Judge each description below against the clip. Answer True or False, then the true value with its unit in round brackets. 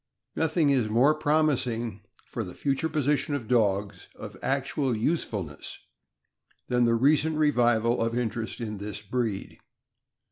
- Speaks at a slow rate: True (120 wpm)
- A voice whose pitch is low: True (120 Hz)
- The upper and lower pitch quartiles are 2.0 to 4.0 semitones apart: False (4.6 semitones)